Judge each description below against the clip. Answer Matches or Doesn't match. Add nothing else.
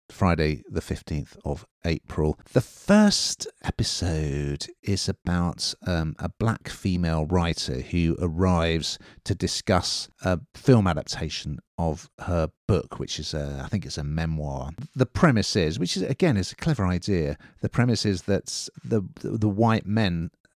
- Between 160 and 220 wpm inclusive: Doesn't match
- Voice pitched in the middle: Doesn't match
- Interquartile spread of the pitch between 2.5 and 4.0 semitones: Doesn't match